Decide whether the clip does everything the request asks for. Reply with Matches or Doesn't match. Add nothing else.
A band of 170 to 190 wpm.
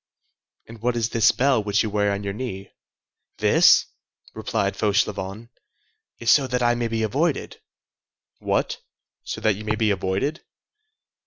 Doesn't match